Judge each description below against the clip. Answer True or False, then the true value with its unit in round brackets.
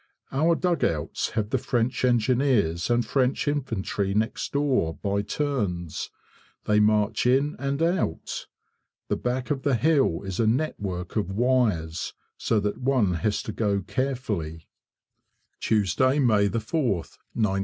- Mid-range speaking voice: False (115 Hz)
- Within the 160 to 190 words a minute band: False (135 wpm)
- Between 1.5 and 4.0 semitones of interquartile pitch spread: False (5.1 semitones)